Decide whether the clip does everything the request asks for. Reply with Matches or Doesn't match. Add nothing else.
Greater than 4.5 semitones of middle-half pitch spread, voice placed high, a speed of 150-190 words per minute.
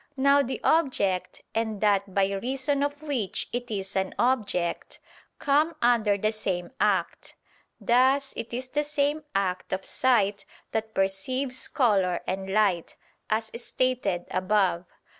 Doesn't match